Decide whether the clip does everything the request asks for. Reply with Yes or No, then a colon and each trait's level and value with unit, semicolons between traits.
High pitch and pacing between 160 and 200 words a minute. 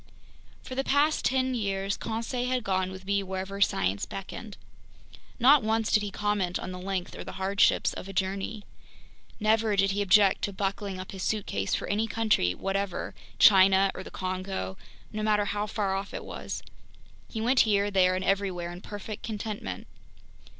Yes: high, 200 Hz; average, 175 wpm